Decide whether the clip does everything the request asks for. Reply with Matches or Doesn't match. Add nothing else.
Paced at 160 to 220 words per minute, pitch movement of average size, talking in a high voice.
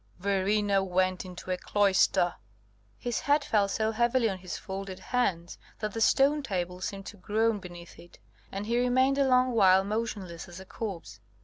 Matches